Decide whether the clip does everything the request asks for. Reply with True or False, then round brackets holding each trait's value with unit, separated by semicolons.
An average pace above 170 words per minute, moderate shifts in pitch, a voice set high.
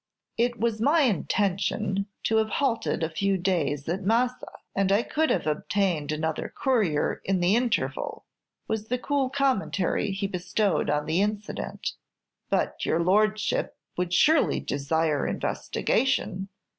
False (135 wpm; 4.8 semitones; 200 Hz)